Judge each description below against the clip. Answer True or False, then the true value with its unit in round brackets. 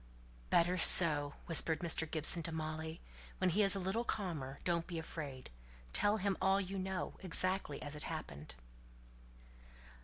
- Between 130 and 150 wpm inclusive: True (145 wpm)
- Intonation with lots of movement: False (3.3 semitones)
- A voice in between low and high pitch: True (170 Hz)